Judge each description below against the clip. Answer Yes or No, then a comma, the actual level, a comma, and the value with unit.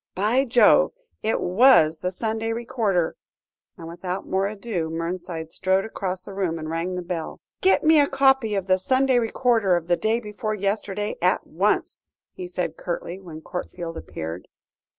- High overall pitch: Yes, high, 195 Hz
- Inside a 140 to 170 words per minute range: Yes, average, 165 wpm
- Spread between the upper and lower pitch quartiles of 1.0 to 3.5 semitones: No, average, 4.7 semitones